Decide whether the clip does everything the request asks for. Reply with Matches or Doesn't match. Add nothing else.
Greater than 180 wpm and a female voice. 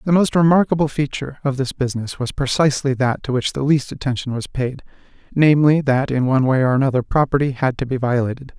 Doesn't match